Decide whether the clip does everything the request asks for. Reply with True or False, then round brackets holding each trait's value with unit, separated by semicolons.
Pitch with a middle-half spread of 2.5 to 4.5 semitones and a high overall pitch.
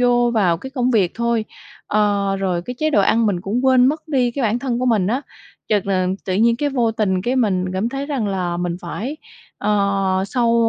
True (4.2 semitones; 225 Hz)